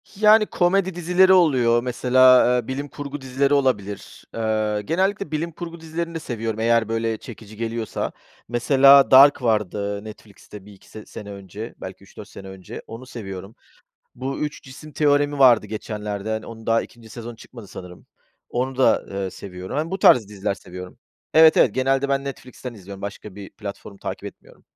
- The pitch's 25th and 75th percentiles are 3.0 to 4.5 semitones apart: No, average, 5.1 semitones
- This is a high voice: No, low, 120 Hz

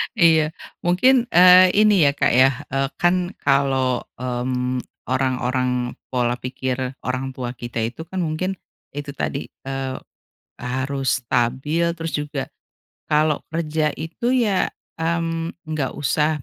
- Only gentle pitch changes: No, average, 4.4 semitones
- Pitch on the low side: No, medium, 145 Hz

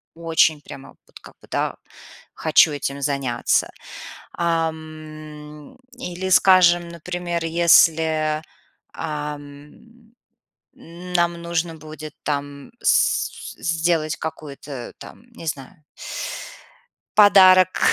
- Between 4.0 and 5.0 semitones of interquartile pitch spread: No, narrow, 2.4 semitones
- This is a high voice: No, medium, 160 Hz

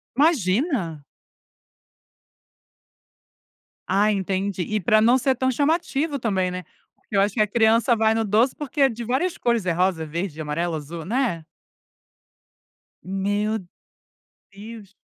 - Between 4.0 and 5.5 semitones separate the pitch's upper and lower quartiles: Yes, average, 4.7 semitones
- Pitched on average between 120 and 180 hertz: No, high, 210 Hz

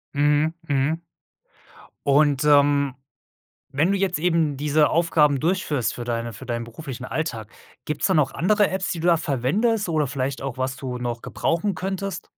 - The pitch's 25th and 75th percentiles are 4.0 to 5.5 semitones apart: Yes, average, 4.3 semitones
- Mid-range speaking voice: Yes, medium, 150 Hz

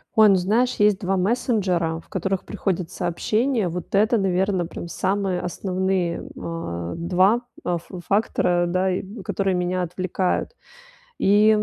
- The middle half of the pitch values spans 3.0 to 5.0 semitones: No, narrow, 2.5 semitones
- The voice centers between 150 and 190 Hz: Yes, medium, 185 Hz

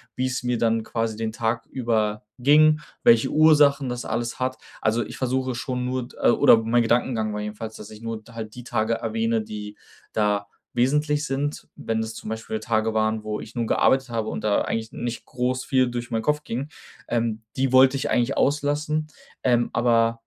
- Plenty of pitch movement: No, narrow, 2.6 semitones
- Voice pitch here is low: Yes, low, 120 Hz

